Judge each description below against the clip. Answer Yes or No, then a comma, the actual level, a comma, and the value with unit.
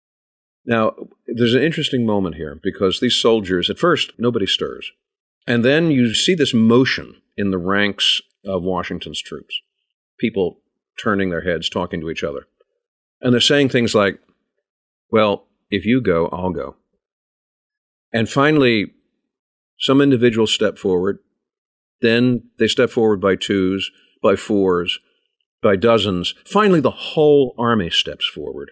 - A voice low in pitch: Yes, low, 120 Hz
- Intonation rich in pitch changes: Yes, wide, 6.9 semitones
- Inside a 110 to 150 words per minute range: Yes, average, 140 wpm